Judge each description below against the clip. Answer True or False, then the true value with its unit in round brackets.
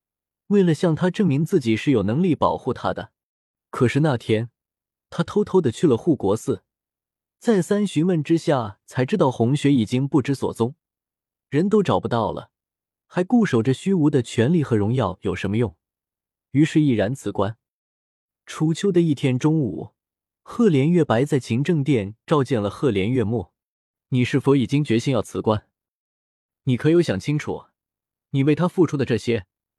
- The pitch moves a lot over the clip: True (6.2 semitones)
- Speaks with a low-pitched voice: True (130 Hz)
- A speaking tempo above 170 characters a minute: True (240 characters per minute)